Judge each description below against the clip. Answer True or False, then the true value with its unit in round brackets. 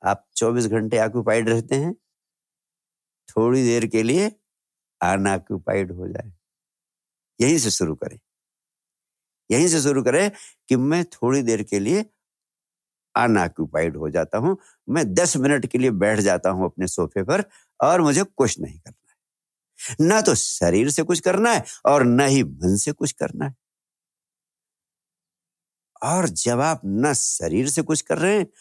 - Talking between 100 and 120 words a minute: False (155 wpm)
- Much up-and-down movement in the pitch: True (6.7 semitones)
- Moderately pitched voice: False (130 Hz)